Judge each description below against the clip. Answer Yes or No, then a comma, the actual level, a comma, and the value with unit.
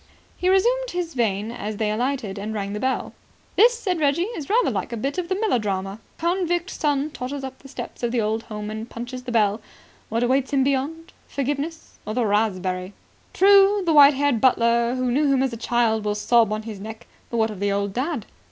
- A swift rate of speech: Yes, fast, 215 wpm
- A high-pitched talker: Yes, very high, 250 Hz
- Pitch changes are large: Yes, wide, 5.7 semitones